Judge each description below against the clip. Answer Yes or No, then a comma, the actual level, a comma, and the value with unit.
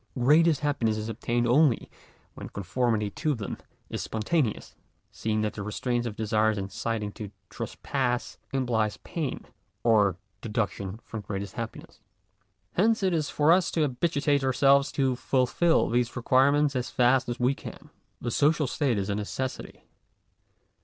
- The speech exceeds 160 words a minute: No, average, 145 wpm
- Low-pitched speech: Yes, low, 120 Hz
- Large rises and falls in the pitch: No, average, 4.7 semitones